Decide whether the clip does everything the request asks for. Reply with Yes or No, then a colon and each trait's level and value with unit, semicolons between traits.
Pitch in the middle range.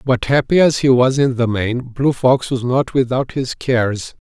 No: low, 130 Hz